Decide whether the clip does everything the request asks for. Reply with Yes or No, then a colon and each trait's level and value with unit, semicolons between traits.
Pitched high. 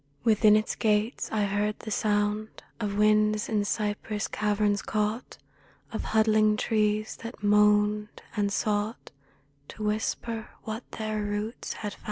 Yes: high, 210 Hz